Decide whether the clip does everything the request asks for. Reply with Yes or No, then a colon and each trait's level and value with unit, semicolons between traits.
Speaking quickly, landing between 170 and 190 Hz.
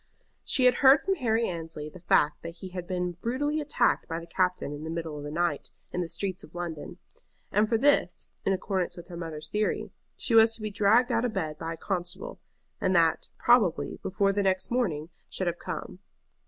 Yes: fast, 210 wpm; medium, 185 Hz